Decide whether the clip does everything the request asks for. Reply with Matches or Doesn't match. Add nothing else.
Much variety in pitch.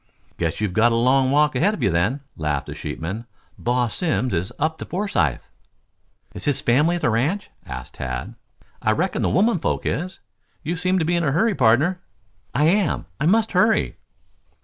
Matches